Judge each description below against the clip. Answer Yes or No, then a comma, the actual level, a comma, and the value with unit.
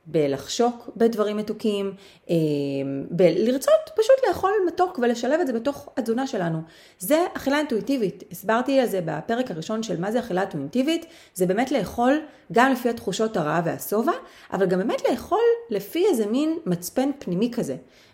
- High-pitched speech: Yes, high, 230 Hz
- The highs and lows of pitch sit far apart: Yes, wide, 6.8 semitones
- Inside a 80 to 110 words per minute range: No, average, 145 wpm